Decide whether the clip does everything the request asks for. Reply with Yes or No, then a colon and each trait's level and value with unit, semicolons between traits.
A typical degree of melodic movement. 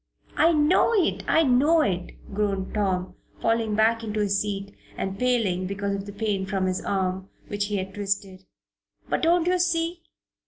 Yes: average, 4.5 semitones